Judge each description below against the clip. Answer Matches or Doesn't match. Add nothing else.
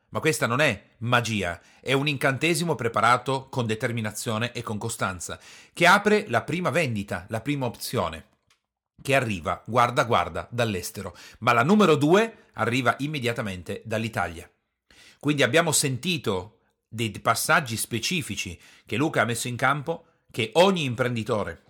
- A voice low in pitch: Matches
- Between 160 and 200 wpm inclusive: Doesn't match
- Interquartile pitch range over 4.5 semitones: Matches